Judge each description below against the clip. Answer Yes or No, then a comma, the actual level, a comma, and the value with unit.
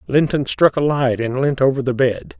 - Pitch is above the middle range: No, low, 135 Hz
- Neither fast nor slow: No, fast, 225 wpm